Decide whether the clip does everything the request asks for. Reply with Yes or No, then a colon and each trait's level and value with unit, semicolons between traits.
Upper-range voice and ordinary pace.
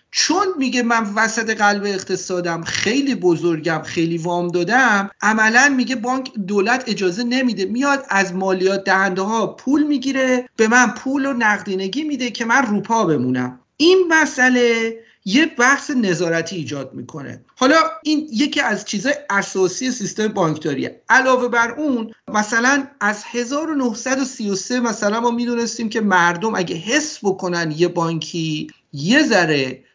Yes: high, 225 Hz; average, 135 wpm